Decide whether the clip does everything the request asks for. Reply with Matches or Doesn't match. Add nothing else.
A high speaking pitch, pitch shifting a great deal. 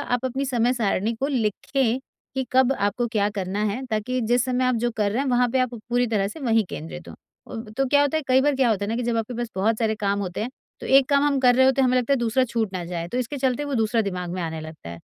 Doesn't match